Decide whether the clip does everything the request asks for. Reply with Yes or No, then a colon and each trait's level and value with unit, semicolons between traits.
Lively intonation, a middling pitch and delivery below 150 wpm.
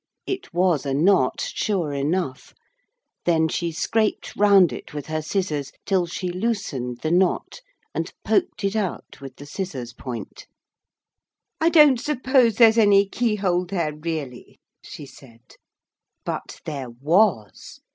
Yes: wide, 6.2 semitones; medium, 175 Hz; slow, 135 wpm